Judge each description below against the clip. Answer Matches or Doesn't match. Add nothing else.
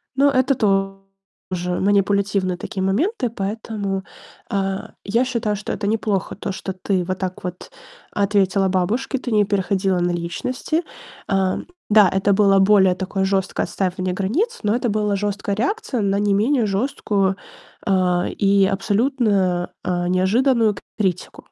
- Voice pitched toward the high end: Matches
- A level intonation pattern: Matches